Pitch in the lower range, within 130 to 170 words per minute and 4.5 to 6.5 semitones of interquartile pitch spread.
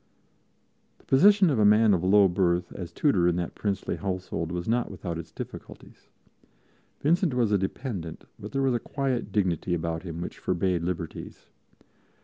Yes: very low, 95 Hz; average, 165 wpm; wide, 5.5 semitones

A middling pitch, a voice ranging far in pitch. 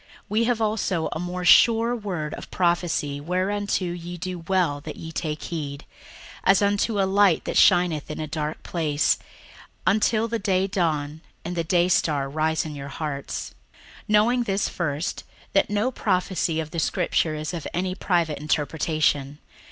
No: medium, 175 Hz; average, 4.0 semitones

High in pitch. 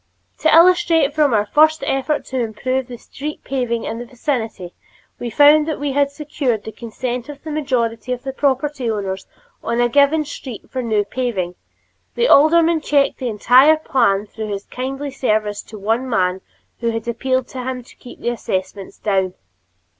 Yes: very high, 255 Hz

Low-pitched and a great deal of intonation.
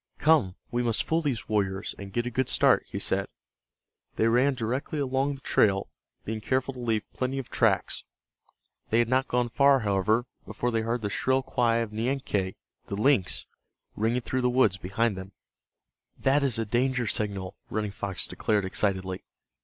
No: low, 115 Hz; average, 4.1 semitones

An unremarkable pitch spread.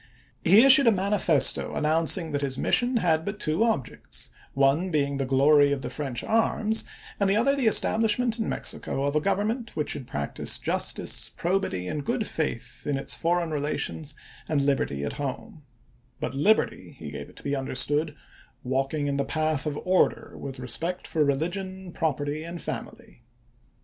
No: wide, 6.1 semitones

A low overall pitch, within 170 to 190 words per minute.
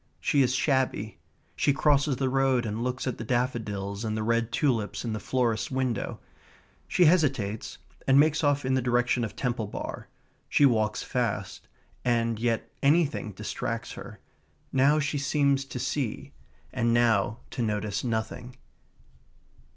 No: low, 125 Hz; average, 150 wpm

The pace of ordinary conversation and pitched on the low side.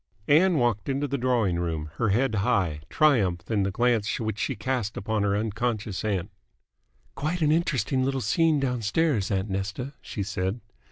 Yes: average, 165 wpm; low, 110 Hz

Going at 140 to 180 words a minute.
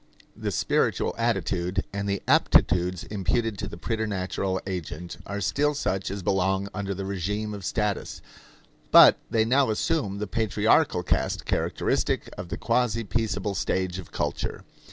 Yes: average, 145 wpm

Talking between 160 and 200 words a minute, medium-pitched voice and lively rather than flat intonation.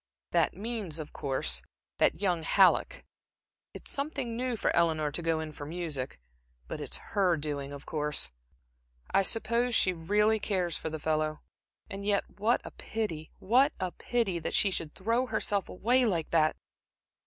Yes: average, 165 wpm; medium, 180 Hz; wide, 5.9 semitones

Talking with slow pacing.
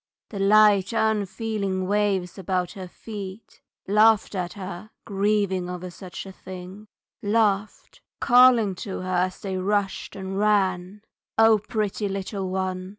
Yes: slow, 130 wpm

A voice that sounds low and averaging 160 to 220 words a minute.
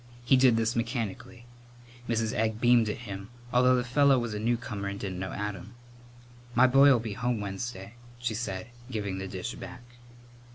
Yes: low, 115 Hz; average, 170 wpm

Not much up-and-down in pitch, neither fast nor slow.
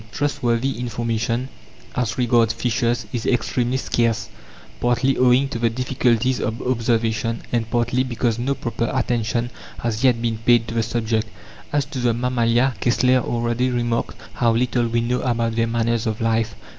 Yes: narrow, 1.5 semitones; average, 155 wpm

